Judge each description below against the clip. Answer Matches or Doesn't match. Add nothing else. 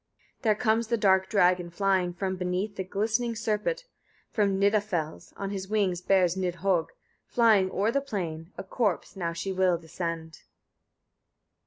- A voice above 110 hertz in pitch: Matches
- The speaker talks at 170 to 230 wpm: Doesn't match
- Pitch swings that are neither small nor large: Matches